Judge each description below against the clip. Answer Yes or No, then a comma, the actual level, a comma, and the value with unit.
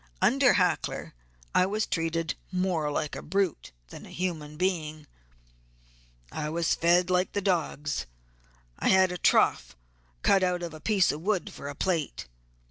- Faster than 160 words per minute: No, average, 150 wpm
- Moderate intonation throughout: Yes, average, 3.2 semitones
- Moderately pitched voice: Yes, medium, 175 Hz